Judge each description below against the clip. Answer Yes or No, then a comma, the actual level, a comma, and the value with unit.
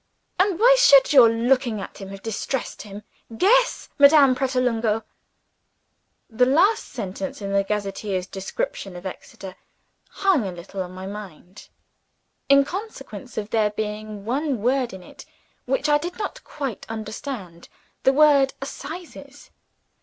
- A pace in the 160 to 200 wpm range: No, average, 140 wpm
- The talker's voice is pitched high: Yes, high, 235 Hz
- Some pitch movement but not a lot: No, wide, 5.9 semitones